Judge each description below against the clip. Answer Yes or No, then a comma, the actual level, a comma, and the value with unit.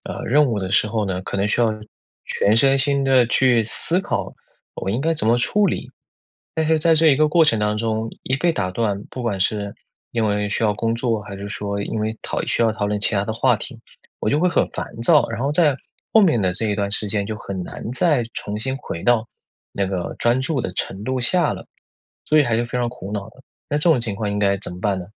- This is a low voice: Yes, low, 115 Hz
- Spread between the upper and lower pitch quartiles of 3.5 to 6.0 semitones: Yes, average, 4.6 semitones